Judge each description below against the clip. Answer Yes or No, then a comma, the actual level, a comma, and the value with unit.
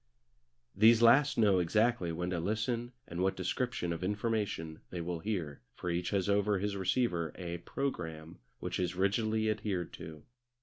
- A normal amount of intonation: Yes, average, 4.1 semitones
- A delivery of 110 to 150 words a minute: No, average, 160 wpm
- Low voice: Yes, very low, 95 Hz